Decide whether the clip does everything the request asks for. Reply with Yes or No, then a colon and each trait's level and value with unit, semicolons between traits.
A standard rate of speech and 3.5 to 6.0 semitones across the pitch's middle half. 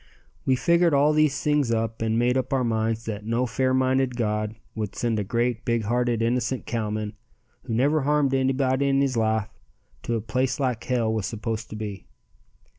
No: average, 190 wpm; average, 2.9 semitones